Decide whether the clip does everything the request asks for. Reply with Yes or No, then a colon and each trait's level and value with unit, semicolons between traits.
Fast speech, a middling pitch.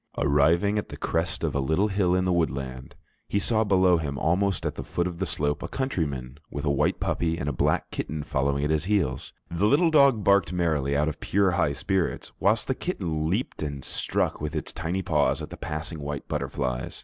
No: fast, 215 wpm; very low, 80 Hz